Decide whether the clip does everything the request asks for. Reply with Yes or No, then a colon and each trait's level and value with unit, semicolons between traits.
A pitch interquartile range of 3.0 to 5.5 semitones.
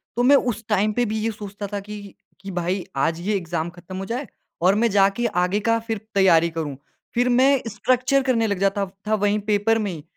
Yes: average, 3.3 semitones